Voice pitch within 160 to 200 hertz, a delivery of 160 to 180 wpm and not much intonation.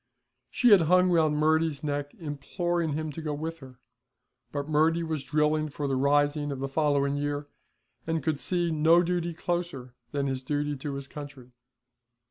No: medium, 150 Hz; average, 170 wpm; narrow, 2.3 semitones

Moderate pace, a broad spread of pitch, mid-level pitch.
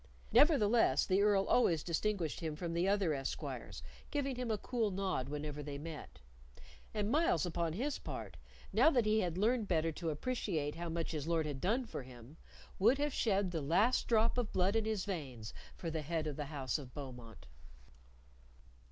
Yes: average, 185 wpm; wide, 6.3 semitones; medium, 175 Hz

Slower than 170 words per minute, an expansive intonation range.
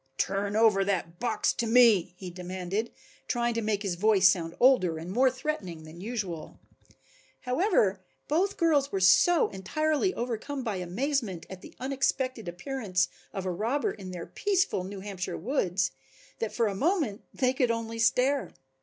Yes: average, 160 wpm; wide, 5.9 semitones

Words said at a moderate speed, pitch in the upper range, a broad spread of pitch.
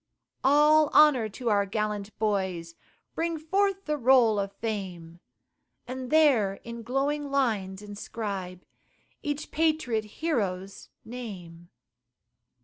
No: slow, 105 wpm; high, 225 Hz; wide, 6.7 semitones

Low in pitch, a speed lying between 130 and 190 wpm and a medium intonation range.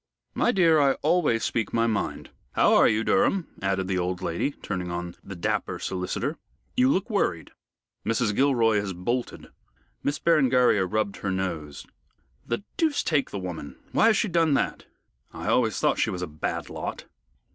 No: low, 115 Hz; average, 170 wpm; wide, 8.6 semitones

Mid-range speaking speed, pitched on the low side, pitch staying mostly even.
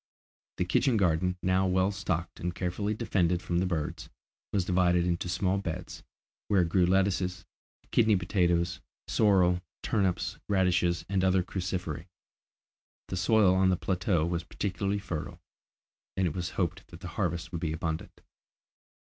Yes: average, 145 wpm; very low, 90 Hz; narrow, 1.7 semitones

